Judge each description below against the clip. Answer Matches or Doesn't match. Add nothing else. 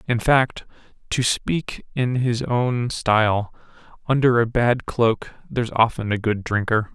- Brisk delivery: Doesn't match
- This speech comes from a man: Matches